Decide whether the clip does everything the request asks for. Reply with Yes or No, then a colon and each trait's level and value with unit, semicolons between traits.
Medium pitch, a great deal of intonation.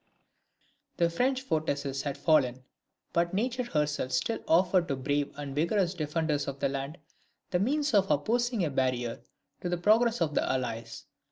Yes: medium, 160 Hz; wide, 6.0 semitones